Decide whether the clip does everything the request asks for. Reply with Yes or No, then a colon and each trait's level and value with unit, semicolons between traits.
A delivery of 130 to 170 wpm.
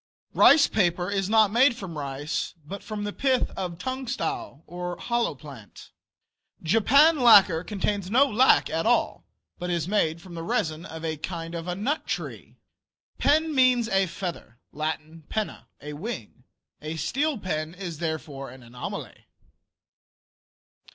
Yes: average, 140 wpm